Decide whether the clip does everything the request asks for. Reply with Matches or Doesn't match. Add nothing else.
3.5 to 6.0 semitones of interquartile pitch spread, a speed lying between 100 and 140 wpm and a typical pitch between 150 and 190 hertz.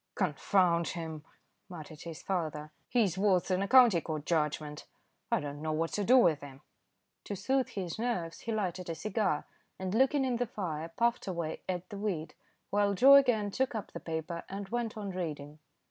Doesn't match